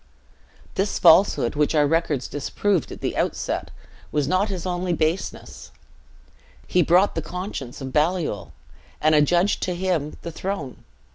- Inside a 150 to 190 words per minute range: No, average, 140 wpm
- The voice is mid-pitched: Yes, medium, 170 Hz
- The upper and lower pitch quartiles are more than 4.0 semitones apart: No, average, 3.6 semitones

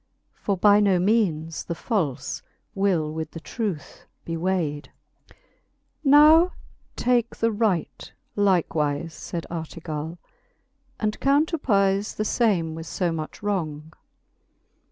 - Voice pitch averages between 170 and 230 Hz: Yes, medium, 185 Hz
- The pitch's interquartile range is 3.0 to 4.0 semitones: No, average, 4.8 semitones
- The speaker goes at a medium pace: No, slow, 115 wpm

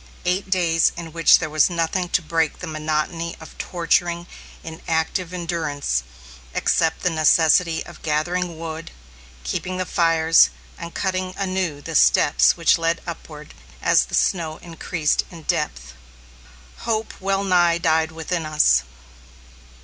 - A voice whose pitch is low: No, medium, 165 Hz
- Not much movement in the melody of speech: Yes, narrow, 2.1 semitones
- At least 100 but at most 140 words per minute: Yes, slow, 135 wpm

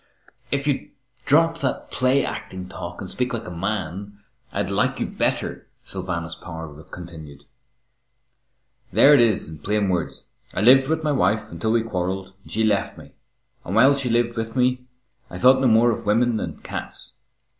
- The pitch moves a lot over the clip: Yes, wide, 5.7 semitones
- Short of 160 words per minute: No, average, 175 wpm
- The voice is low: Yes, low, 110 Hz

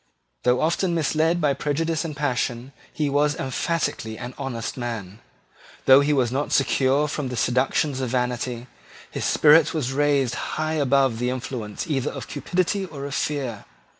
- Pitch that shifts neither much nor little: Yes, average, 3.3 semitones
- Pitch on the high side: No, medium, 140 Hz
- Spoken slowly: No, average, 160 wpm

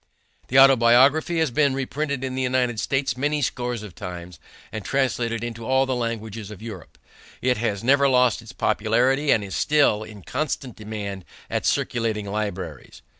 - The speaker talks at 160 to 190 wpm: Yes, average, 165 wpm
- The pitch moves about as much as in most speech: Yes, average, 3.8 semitones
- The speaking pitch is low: Yes, low, 120 Hz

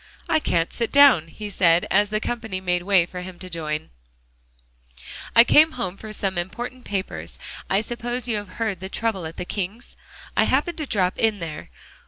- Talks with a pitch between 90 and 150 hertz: No, high, 200 Hz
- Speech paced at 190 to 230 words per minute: Yes, average, 195 wpm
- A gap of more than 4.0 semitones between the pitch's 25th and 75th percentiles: Yes, average, 4.5 semitones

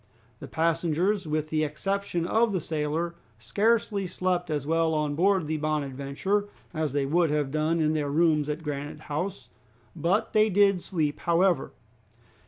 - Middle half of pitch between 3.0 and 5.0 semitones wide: Yes, average, 3.6 semitones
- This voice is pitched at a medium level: Yes, medium, 160 Hz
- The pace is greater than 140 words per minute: Yes, average, 155 wpm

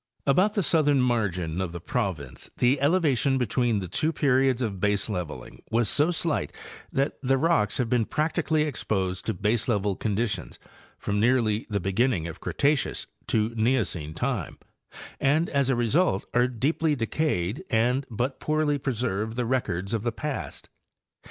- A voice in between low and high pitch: No, low, 120 Hz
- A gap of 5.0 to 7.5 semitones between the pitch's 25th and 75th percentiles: Yes, average, 5.3 semitones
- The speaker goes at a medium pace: Yes, average, 150 wpm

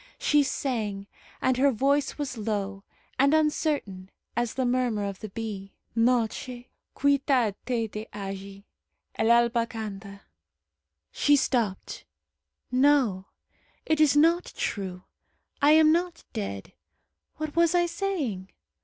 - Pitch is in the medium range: No, high, 240 Hz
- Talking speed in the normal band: No, slow, 120 wpm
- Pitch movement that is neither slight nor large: No, wide, 6.1 semitones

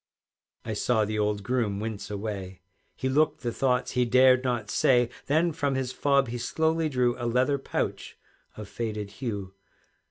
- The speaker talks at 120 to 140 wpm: No, average, 165 wpm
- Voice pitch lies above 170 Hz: No, low, 120 Hz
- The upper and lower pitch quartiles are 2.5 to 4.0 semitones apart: Yes, average, 3.7 semitones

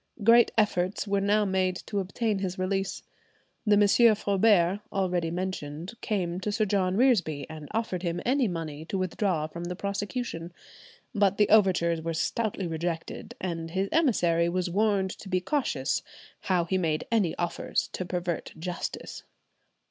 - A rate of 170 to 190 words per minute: No, average, 155 wpm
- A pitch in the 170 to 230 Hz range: Yes, medium, 185 Hz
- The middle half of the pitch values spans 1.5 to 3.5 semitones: Yes, average, 3.2 semitones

